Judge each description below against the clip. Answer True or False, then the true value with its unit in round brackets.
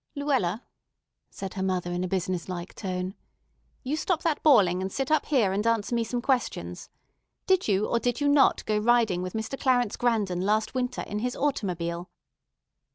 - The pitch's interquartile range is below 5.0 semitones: False (5.6 semitones)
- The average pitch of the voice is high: True (220 Hz)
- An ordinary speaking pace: True (180 wpm)